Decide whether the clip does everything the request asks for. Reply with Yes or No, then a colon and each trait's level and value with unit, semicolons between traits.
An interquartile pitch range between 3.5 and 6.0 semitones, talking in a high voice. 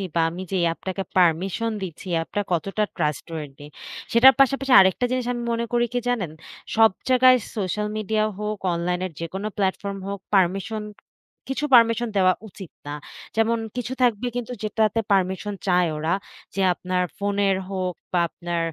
Yes: average, 4.2 semitones; high, 195 Hz